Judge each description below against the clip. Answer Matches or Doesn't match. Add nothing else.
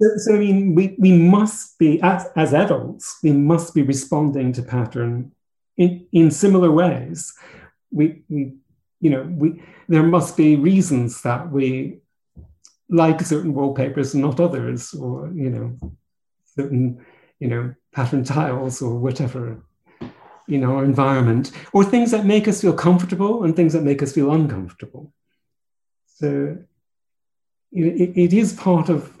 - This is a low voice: Doesn't match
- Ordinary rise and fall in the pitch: Matches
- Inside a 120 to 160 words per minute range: Matches